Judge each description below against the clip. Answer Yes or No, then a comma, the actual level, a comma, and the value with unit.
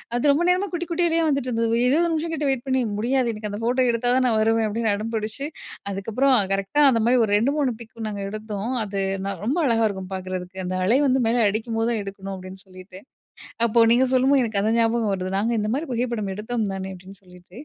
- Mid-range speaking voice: No, high, 225 Hz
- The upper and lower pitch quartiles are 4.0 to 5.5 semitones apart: Yes, average, 4.3 semitones